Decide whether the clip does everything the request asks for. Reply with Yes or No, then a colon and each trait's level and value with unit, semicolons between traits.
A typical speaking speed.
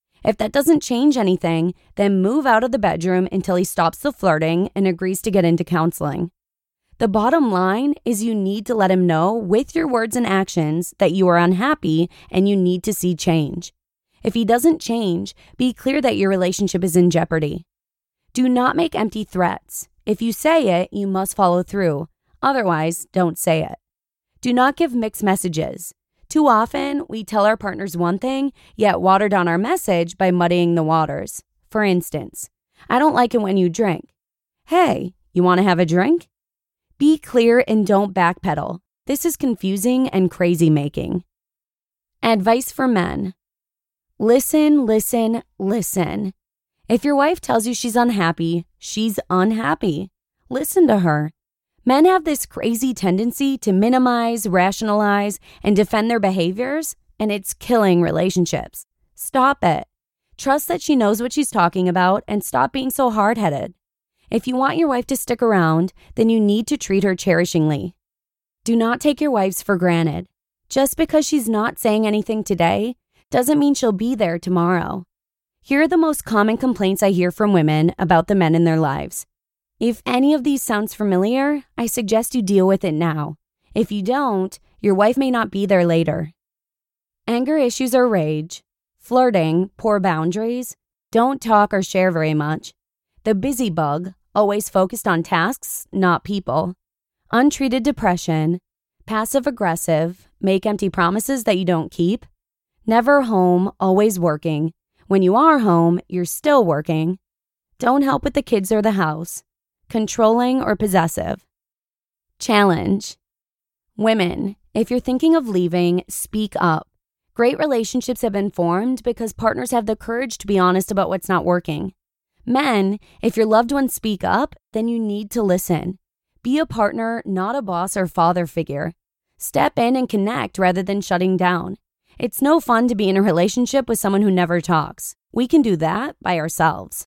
Yes: average, 165 wpm